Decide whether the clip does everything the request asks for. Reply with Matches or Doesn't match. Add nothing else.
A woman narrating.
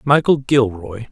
Doesn't match